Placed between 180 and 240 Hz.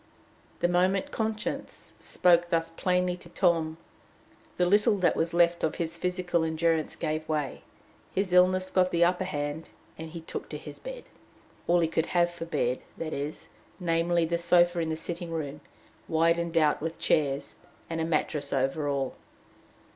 No: medium, 170 Hz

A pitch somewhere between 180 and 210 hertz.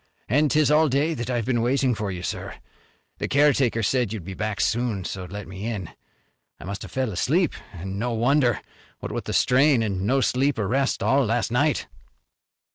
No: low, 120 Hz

